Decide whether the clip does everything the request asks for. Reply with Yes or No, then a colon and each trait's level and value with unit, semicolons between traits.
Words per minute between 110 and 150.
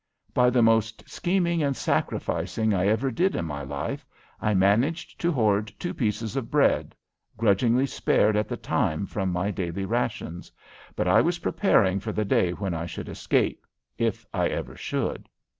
No: average, 170 wpm